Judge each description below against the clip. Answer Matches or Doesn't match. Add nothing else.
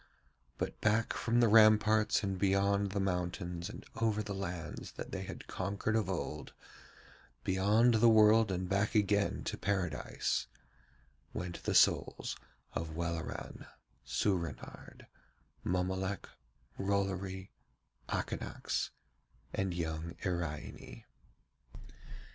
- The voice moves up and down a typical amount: Matches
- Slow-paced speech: Matches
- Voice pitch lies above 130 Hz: Doesn't match